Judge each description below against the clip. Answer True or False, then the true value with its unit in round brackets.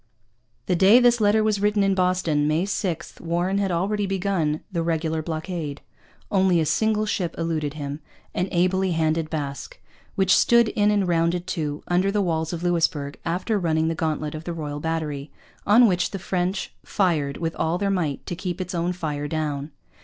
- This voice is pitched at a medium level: True (175 Hz)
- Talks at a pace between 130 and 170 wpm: False (185 wpm)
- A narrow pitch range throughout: False (3.4 semitones)